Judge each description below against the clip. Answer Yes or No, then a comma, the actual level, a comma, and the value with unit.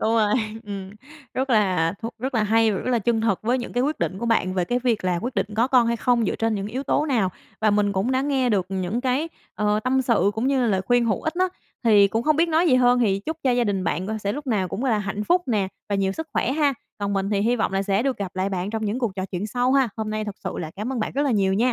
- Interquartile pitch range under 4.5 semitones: Yes, average, 4.1 semitones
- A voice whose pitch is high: Yes, high, 220 Hz